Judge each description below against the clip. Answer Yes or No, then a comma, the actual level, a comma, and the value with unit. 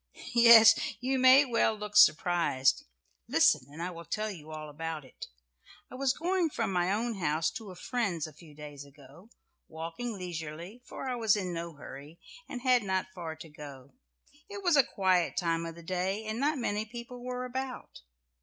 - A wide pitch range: Yes, wide, 7.0 semitones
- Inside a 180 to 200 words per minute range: Yes, average, 185 wpm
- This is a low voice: No, medium, 185 Hz